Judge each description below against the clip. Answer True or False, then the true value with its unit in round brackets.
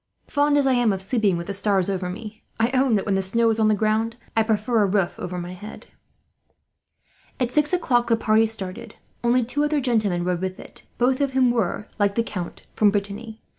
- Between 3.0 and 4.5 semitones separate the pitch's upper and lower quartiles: True (3.5 semitones)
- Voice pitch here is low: False (220 Hz)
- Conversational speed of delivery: False (220 wpm)